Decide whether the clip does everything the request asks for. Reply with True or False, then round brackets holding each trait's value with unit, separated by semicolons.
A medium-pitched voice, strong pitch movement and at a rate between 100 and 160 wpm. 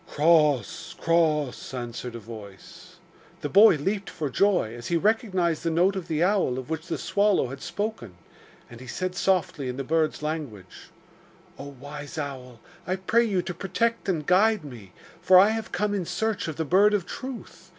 False (165 Hz; 6.3 semitones; 180 wpm)